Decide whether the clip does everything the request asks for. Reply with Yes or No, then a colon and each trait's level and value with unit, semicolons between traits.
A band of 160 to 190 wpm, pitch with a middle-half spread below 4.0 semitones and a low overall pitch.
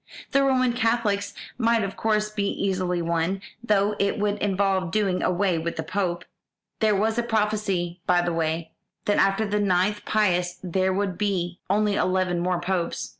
No: average, 170 wpm; average, 2.9 semitones; high, 195 Hz